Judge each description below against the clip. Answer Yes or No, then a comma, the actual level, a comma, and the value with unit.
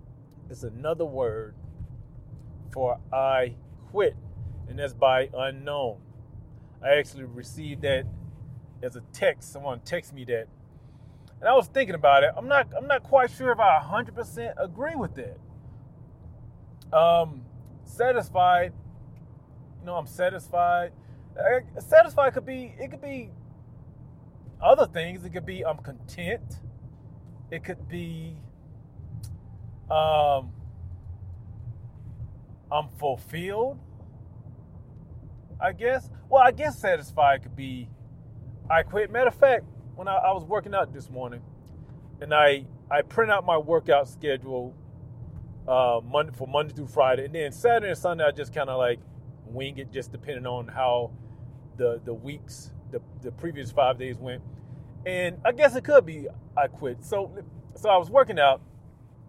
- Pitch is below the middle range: Yes, low, 130 Hz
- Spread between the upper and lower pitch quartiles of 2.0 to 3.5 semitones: No, average, 5.1 semitones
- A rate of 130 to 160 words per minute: Yes, average, 140 wpm